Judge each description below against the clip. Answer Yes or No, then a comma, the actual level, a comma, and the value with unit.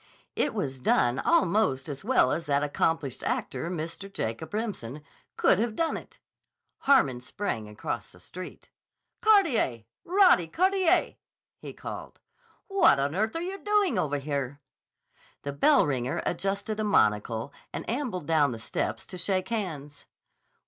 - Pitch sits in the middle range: Yes, medium, 165 Hz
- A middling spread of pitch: No, wide, 8.7 semitones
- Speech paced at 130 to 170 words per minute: Yes, average, 140 wpm